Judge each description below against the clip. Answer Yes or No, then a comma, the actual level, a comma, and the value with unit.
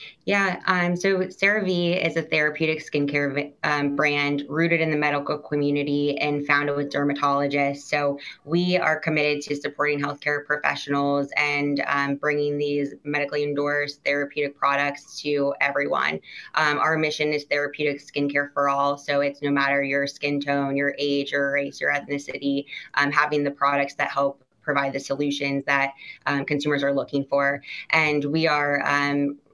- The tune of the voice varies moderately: No, narrow, 0.8 semitones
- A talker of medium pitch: Yes, medium, 145 Hz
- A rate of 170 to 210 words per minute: No, average, 160 wpm